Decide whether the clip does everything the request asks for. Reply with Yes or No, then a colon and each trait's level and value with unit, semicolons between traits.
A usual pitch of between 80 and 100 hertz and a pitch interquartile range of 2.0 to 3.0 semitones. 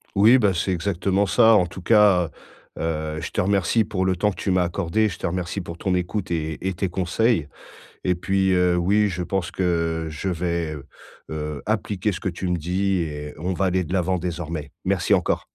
Yes: very low, 90 Hz; narrow, 2.6 semitones